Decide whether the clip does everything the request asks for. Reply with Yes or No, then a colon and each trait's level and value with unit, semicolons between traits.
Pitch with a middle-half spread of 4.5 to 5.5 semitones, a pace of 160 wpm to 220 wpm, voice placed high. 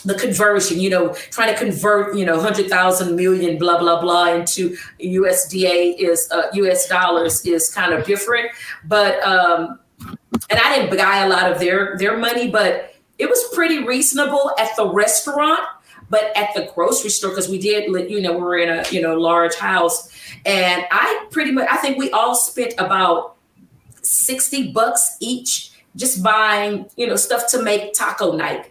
Yes: average, 4.9 semitones; average, 180 wpm; high, 200 Hz